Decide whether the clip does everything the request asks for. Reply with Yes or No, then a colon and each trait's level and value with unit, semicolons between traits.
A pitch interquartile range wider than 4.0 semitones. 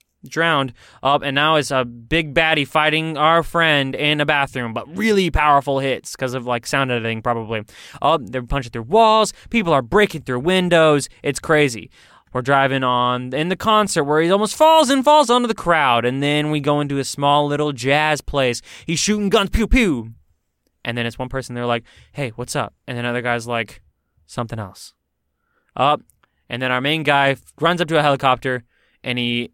Yes: average, 4.8 semitones